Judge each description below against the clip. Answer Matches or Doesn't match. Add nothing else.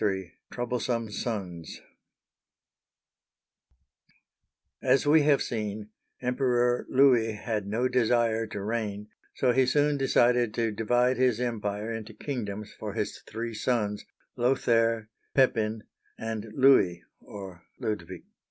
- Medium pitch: Doesn't match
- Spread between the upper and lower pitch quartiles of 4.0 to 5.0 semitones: Doesn't match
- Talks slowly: Matches